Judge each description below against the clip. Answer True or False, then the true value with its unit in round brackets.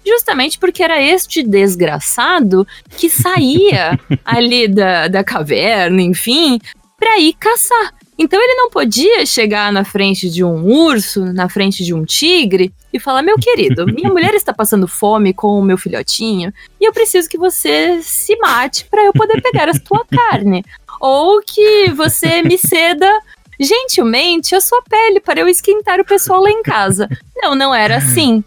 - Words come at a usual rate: True (165 wpm)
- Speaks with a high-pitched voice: True (310 Hz)